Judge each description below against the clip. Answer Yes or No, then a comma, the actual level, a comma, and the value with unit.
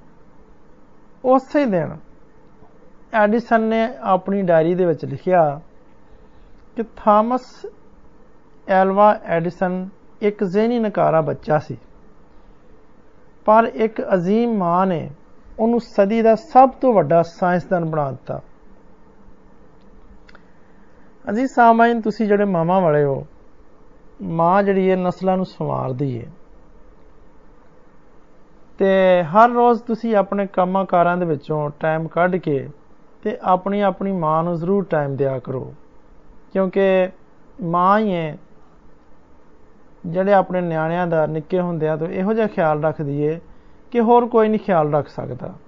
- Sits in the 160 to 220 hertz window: Yes, medium, 185 Hz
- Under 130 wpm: Yes, average, 115 wpm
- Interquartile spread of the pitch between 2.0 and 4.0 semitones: No, average, 5.1 semitones